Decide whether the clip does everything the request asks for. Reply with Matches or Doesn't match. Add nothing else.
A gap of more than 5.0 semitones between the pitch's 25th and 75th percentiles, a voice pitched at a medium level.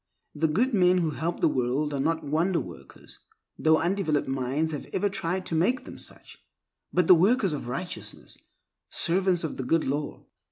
Doesn't match